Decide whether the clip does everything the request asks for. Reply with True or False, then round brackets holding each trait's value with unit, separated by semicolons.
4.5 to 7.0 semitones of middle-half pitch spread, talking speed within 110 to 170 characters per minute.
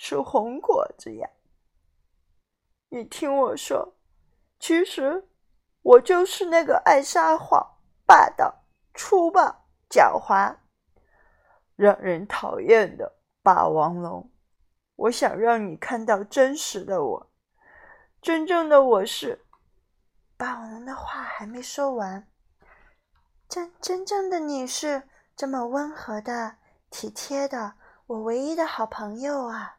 False (7.8 semitones; 160 characters per minute)